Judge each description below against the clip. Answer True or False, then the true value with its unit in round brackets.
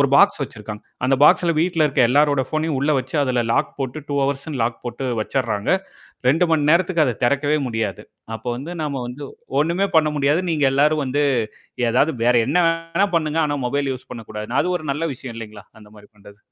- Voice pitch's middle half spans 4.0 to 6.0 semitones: True (4.3 semitones)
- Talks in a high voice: False (140 Hz)